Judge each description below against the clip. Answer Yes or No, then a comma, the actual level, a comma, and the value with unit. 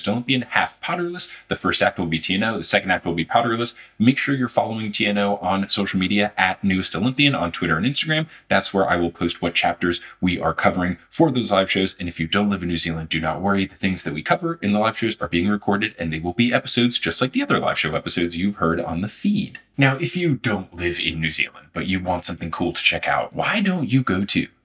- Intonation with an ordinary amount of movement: No, wide, 5.8 semitones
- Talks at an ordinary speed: No, fast, 255 wpm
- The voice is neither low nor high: No, low, 100 Hz